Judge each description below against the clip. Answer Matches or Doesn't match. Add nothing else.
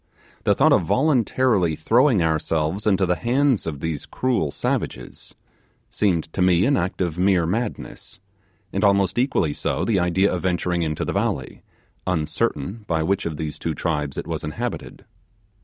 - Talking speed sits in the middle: Matches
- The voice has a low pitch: Matches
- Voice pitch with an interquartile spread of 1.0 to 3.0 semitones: Doesn't match